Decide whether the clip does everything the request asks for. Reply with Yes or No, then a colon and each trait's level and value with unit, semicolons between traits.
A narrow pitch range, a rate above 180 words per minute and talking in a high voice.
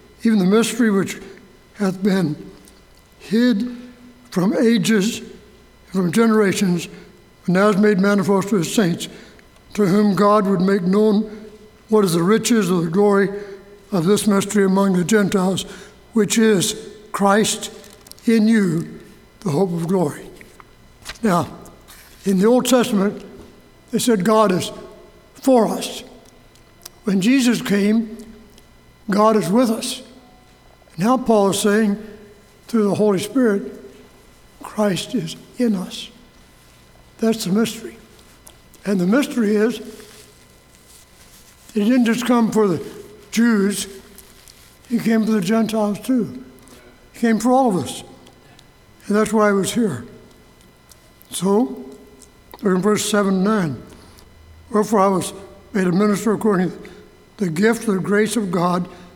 No: narrow, 2.3 semitones; slow, 135 wpm; high, 205 Hz